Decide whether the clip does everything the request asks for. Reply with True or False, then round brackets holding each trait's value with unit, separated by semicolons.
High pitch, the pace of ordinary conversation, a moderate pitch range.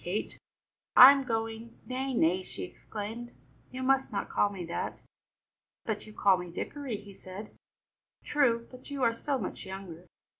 True (225 Hz; 165 wpm; 4.8 semitones)